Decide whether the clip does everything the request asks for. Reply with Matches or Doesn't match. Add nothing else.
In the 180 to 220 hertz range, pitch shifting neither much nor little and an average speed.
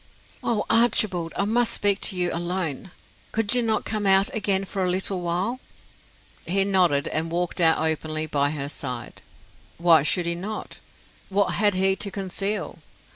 Matches